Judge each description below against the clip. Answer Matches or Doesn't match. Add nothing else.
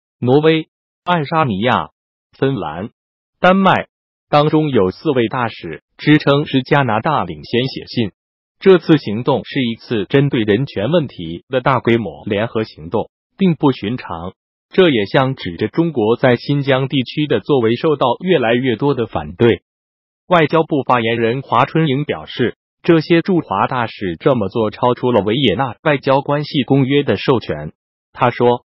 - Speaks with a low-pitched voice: Matches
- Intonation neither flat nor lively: Matches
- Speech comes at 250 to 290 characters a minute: Doesn't match